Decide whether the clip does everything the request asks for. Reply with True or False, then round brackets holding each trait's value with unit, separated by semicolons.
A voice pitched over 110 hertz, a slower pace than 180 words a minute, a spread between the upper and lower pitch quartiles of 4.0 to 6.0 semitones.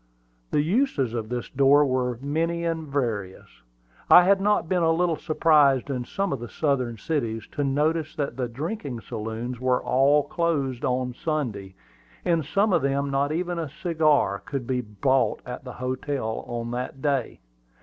True (140 Hz; 170 wpm; 4.5 semitones)